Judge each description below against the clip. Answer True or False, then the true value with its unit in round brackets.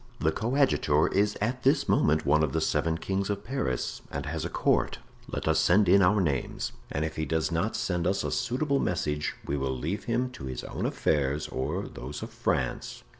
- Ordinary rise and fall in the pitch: False (6.0 semitones)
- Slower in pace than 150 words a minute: False (205 wpm)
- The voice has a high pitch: False (85 Hz)